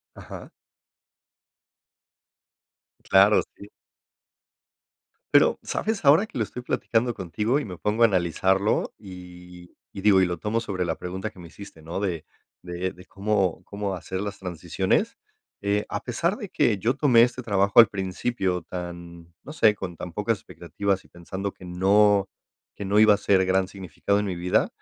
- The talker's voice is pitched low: Yes, low, 100 Hz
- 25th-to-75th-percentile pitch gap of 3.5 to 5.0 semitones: No, average, 2.9 semitones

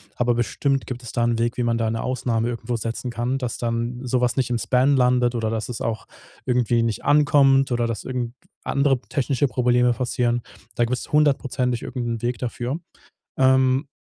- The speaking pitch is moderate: No, low, 125 Hz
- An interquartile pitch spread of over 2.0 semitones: No, narrow, 1.7 semitones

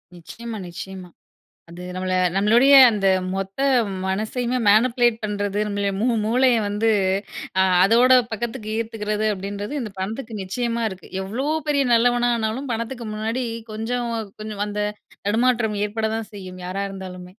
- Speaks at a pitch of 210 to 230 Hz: Yes, high, 215 Hz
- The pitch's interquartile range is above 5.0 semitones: No, average, 3.1 semitones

